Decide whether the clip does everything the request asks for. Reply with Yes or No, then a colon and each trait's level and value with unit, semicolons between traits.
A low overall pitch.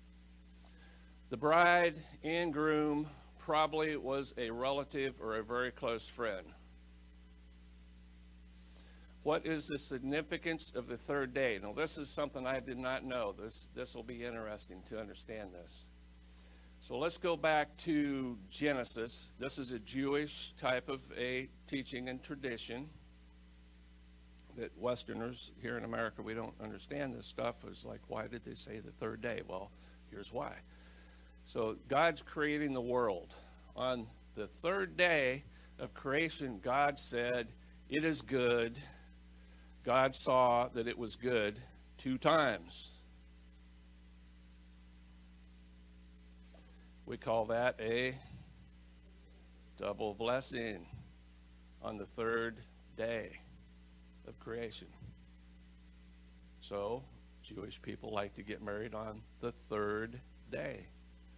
Yes: low, 110 Hz